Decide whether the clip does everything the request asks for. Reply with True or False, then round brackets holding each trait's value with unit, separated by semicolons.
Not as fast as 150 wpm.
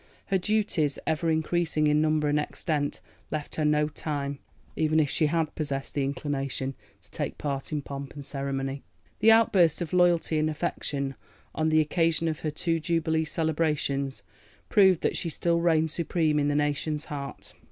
False (170 wpm)